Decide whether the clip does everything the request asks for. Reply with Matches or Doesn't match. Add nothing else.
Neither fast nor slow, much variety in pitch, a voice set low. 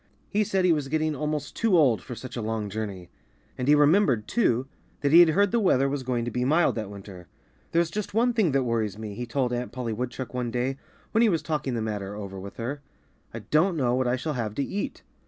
Doesn't match